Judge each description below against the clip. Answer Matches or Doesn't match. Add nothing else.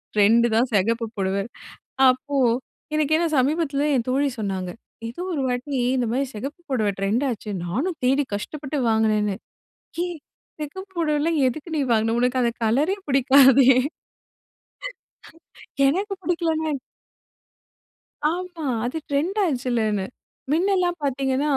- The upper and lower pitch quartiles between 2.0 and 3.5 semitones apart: Doesn't match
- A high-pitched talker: Matches